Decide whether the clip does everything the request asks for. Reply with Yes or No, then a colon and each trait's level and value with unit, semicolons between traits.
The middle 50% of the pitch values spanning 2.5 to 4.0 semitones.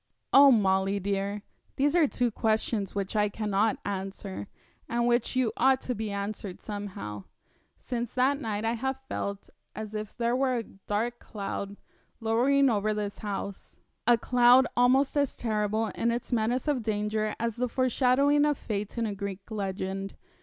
Yes: average, 3.5 semitones